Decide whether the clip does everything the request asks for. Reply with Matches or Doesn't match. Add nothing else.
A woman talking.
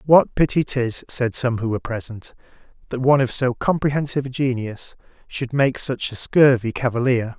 Doesn't match